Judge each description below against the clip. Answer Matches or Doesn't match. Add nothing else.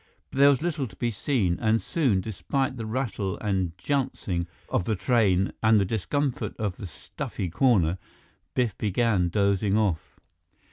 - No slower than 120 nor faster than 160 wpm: Matches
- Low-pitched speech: Matches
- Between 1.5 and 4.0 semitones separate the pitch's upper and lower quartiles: Doesn't match